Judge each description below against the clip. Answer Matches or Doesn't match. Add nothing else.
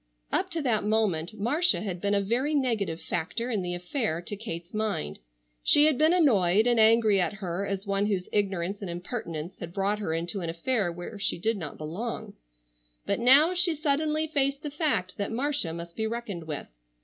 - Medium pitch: Doesn't match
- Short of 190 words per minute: Doesn't match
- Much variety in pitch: Matches